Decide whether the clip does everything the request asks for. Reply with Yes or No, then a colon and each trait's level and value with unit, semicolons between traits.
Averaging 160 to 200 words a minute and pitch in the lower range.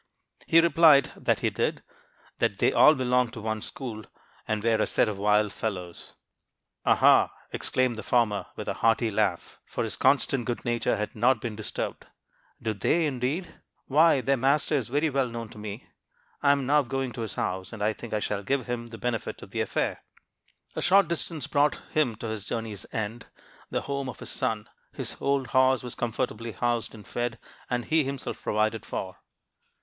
Yes: average, 190 wpm; low, 120 Hz